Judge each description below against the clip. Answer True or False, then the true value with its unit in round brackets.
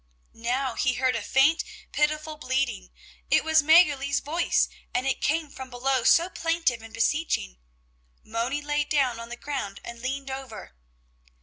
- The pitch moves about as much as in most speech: True (3.7 semitones)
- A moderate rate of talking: True (150 wpm)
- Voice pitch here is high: True (270 Hz)